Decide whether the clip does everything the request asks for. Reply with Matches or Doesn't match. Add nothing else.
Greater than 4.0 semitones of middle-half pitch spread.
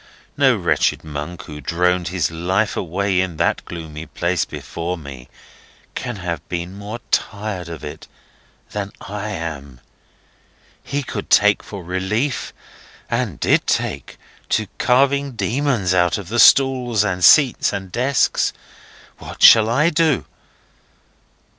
Matches